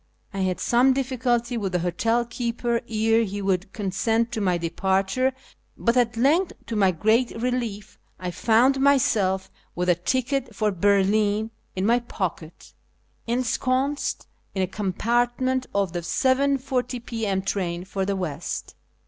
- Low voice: No, high, 225 Hz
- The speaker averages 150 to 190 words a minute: No, average, 140 wpm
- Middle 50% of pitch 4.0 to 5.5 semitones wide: Yes, average, 4.4 semitones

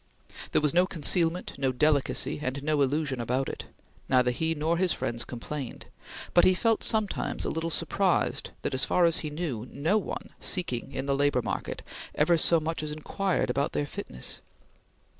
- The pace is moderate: Yes, average, 180 wpm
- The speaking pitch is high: No, medium, 150 Hz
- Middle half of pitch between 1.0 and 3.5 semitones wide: No, average, 4.0 semitones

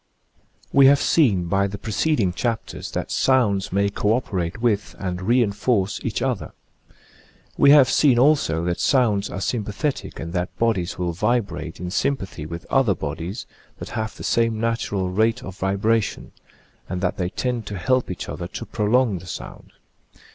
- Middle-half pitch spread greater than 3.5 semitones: Yes, average, 4.7 semitones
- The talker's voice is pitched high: No, low, 105 Hz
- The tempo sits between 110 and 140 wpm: No, average, 165 wpm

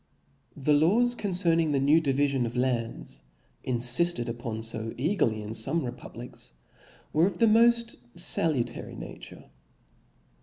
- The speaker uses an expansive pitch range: Yes, wide, 6.4 semitones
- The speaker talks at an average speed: No, slow, 125 wpm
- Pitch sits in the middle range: Yes, medium, 145 Hz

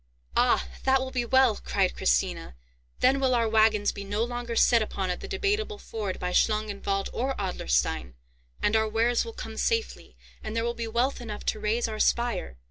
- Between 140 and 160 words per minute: No, average, 190 wpm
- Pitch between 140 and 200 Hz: No, high, 225 Hz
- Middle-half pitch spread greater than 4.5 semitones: No, average, 3.1 semitones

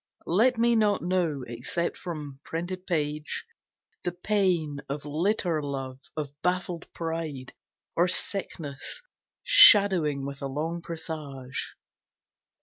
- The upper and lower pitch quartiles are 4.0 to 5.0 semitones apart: Yes, average, 4.3 semitones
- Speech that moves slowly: Yes, slow, 110 wpm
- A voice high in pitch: No, medium, 165 Hz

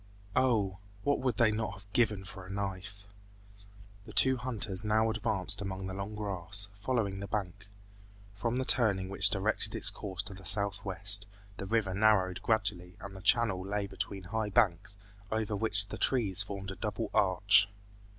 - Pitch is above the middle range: No, low, 100 Hz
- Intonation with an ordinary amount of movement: No, narrow, 2.1 semitones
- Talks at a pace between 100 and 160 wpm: No, average, 170 wpm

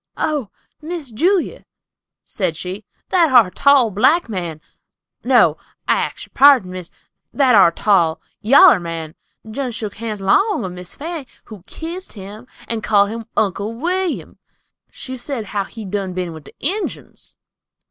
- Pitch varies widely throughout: Yes, wide, 7.0 semitones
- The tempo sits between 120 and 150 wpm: Yes, average, 145 wpm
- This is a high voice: Yes, high, 220 Hz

